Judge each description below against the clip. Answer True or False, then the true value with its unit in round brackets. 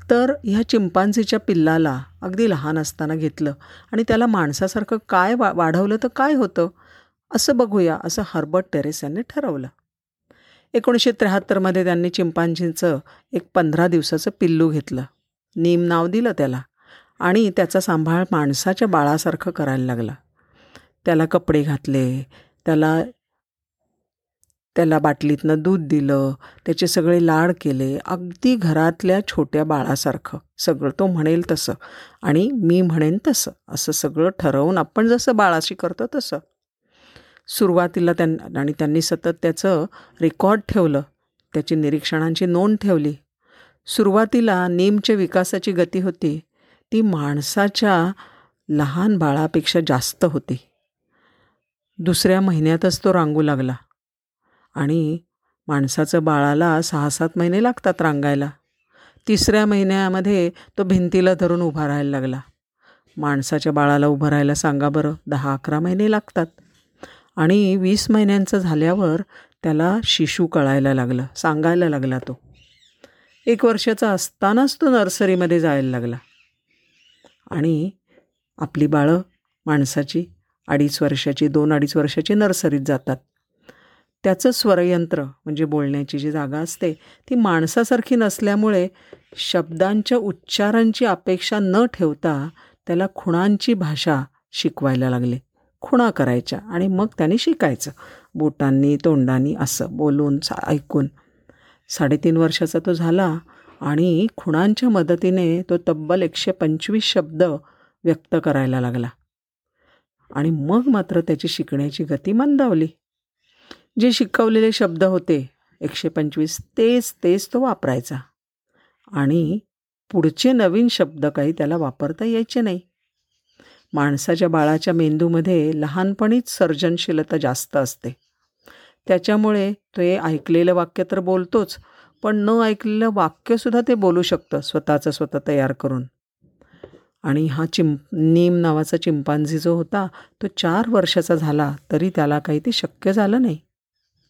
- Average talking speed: True (115 wpm)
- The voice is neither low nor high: True (170 Hz)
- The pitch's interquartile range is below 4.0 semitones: False (4.5 semitones)